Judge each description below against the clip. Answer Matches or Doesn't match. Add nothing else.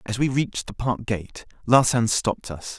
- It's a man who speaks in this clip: Matches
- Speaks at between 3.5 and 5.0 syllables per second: Matches